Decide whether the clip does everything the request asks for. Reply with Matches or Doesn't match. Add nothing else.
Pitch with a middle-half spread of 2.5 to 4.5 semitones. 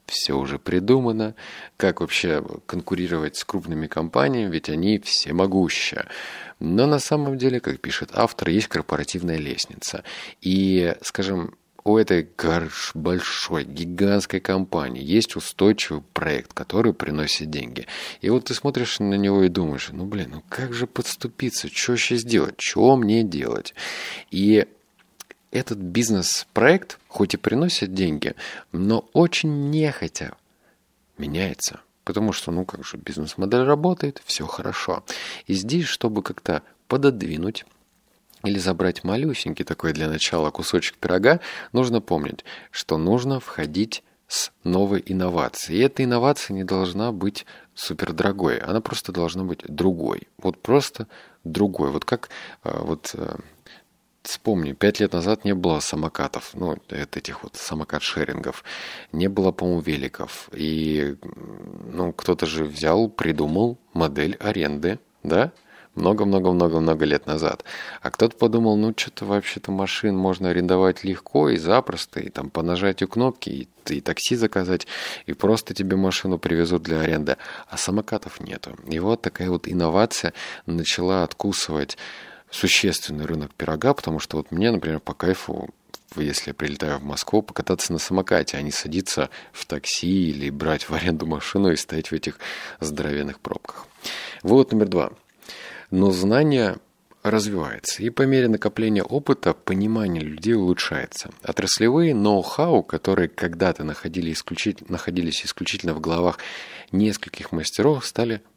Doesn't match